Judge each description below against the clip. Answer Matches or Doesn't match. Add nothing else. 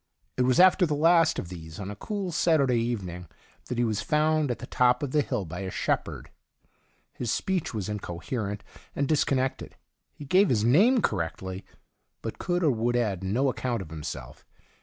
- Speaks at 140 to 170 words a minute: Doesn't match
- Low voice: Matches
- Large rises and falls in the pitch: Matches